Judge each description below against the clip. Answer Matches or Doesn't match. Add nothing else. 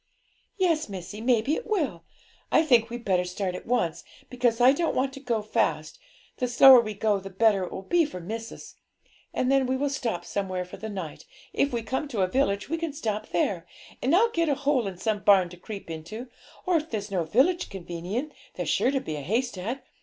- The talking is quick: Matches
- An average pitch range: Doesn't match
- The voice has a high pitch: Matches